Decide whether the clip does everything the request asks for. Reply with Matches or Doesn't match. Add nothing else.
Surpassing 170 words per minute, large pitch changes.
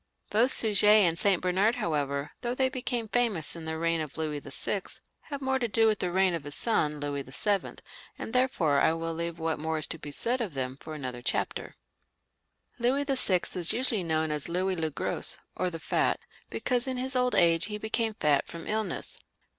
Matches